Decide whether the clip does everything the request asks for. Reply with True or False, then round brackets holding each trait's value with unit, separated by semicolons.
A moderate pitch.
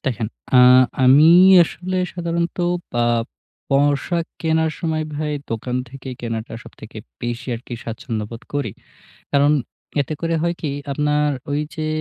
True (145 Hz)